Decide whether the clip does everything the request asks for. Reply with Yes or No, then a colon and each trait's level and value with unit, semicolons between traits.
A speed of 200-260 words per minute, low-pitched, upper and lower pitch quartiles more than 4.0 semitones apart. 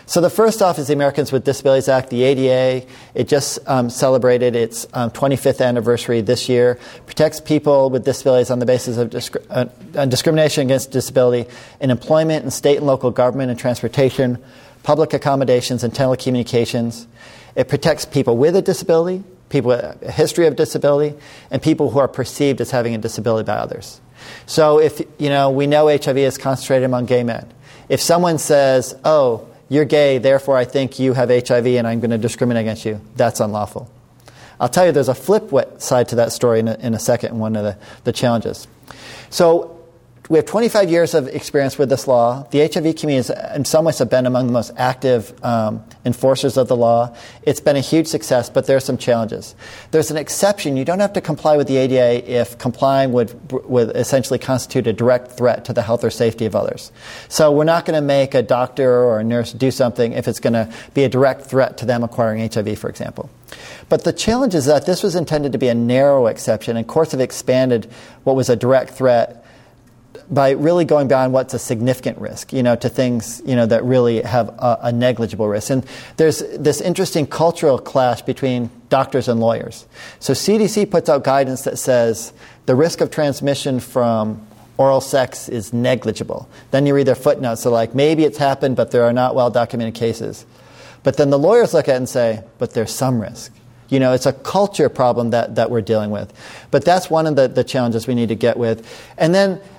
No: fast, 205 wpm; low, 130 Hz; average, 3.0 semitones